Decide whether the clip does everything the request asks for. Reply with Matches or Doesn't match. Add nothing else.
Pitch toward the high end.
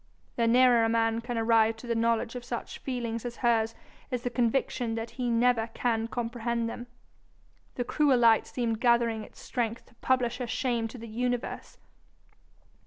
Matches